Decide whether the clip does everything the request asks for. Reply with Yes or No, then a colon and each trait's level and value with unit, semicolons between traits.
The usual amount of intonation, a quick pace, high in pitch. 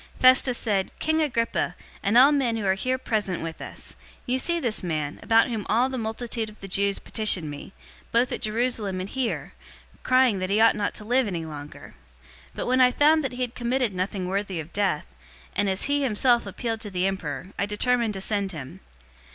Yes: average, 4.6 semitones; fast, 210 wpm; high, 215 Hz